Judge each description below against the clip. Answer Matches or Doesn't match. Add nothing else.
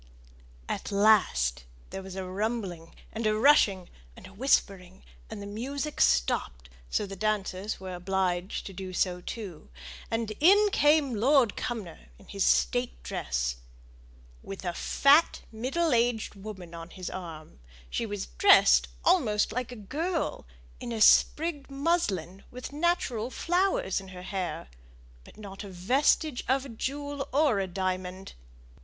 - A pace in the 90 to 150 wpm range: Matches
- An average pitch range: Doesn't match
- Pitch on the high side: Matches